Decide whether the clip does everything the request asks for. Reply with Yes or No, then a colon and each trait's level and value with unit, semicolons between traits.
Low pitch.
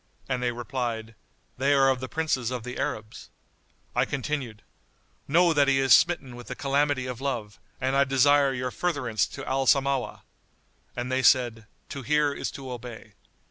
Yes: low, 130 Hz